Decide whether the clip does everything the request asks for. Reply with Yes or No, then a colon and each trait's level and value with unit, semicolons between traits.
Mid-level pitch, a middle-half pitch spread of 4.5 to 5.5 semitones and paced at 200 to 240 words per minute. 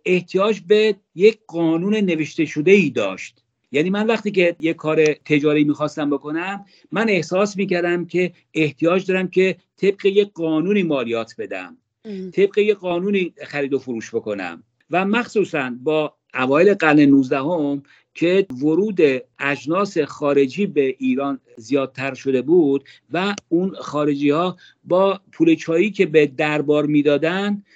No: medium, 165 Hz; average, 4.8 semitones; slow, 135 wpm